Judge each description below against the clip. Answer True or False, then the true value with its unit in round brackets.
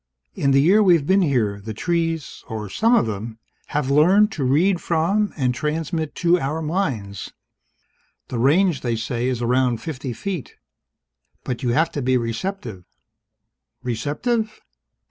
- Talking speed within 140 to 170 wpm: True (150 wpm)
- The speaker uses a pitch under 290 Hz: True (140 Hz)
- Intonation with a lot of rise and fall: True (6.5 semitones)